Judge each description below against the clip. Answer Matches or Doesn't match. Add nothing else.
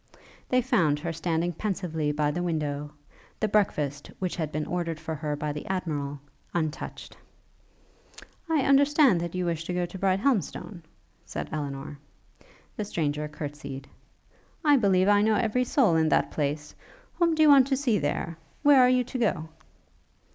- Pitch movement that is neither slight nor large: Doesn't match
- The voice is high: Doesn't match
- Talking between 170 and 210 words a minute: Doesn't match